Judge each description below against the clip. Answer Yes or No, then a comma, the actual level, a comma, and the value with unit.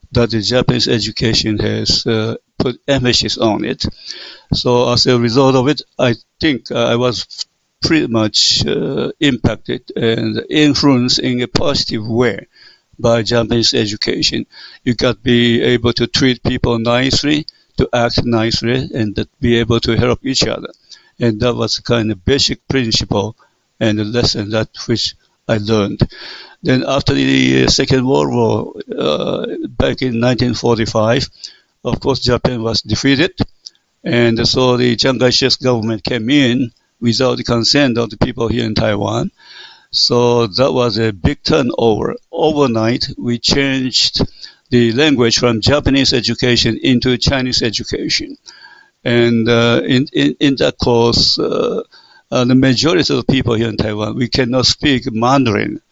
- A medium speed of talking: Yes, average, 145 wpm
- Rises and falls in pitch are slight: Yes, narrow, 2.2 semitones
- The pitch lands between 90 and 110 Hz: No, low, 120 Hz